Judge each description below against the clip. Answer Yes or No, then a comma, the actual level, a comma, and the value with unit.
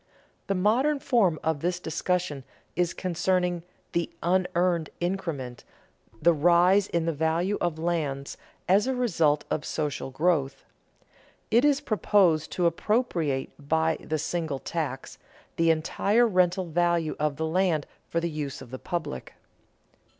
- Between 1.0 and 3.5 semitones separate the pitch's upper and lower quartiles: Yes, average, 2.9 semitones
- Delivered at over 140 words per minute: No, slow, 135 wpm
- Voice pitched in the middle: Yes, medium, 170 Hz